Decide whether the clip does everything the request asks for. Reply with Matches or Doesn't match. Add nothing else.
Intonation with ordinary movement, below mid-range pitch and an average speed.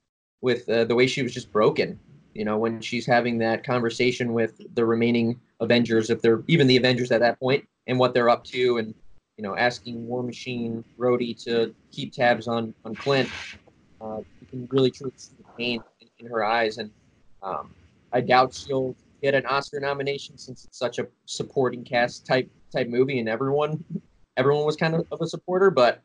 Doesn't match